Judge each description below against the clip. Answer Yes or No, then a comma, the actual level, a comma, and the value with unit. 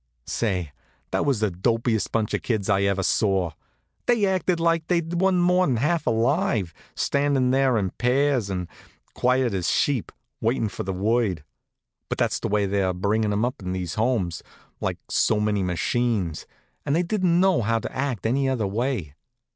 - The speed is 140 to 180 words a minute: Yes, average, 170 wpm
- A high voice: No, low, 115 Hz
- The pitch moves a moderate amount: No, wide, 6.2 semitones